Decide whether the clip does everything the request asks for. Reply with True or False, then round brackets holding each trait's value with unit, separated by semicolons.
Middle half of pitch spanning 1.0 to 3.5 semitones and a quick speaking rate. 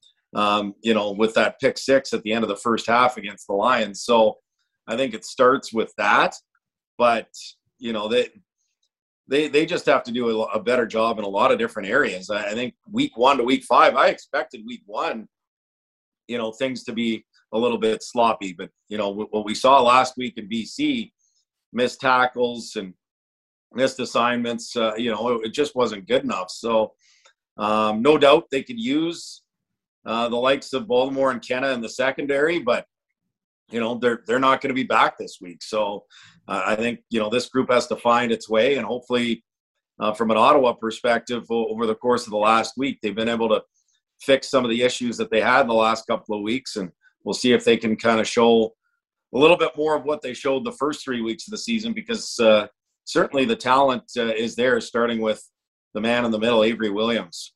True (3.1 semitones; 210 wpm)